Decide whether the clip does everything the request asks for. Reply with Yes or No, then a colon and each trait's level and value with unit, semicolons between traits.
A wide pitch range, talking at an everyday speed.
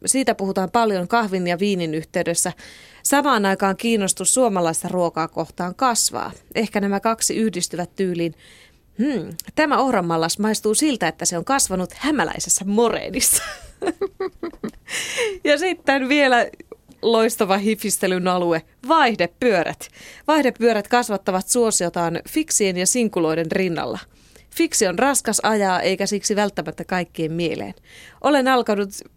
Yes: wide, 6.1 semitones; average, 115 wpm